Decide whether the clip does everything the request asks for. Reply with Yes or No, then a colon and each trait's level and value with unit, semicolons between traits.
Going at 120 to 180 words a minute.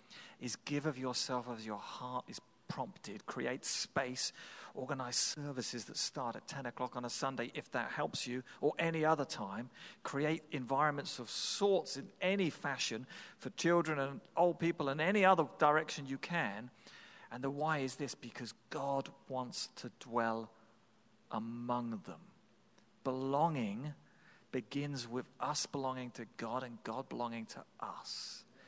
Yes: average, 150 wpm